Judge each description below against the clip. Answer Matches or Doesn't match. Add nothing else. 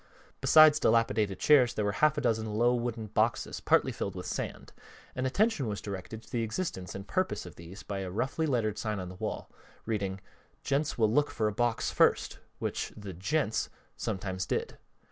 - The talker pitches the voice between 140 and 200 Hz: Doesn't match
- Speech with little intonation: Doesn't match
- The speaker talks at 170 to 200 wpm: Matches